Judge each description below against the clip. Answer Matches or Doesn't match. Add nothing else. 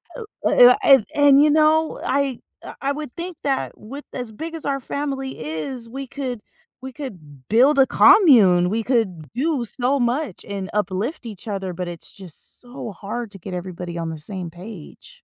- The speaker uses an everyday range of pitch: Doesn't match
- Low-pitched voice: Doesn't match